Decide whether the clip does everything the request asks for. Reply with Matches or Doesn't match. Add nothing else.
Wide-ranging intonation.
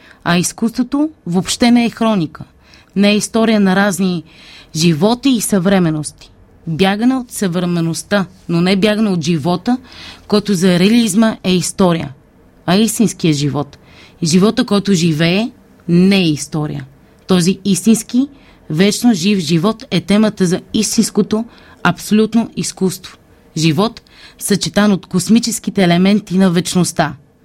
Doesn't match